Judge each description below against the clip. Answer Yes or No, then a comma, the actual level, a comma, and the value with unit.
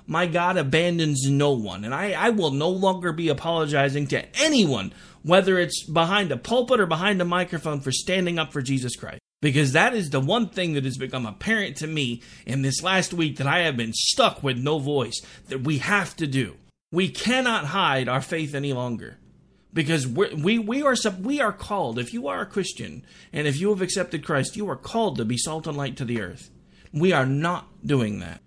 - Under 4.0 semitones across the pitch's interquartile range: No, wide, 5.5 semitones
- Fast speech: Yes, fast, 215 wpm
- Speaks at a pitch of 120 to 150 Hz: No, medium, 160 Hz